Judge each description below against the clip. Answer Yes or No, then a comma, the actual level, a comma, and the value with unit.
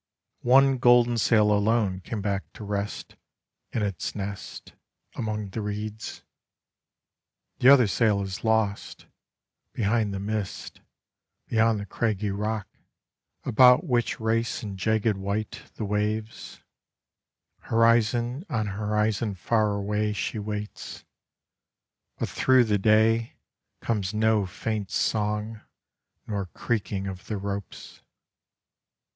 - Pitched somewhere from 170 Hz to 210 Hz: No, low, 105 Hz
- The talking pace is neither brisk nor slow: No, slow, 110 wpm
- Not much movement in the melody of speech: Yes, narrow, 1.9 semitones